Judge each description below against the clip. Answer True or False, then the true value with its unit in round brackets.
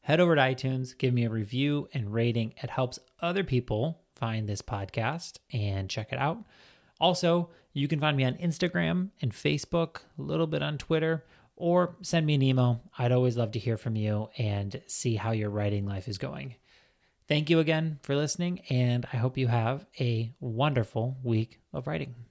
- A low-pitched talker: True (130 Hz)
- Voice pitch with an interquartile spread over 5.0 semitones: True (5.6 semitones)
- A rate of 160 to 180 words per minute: False (190 wpm)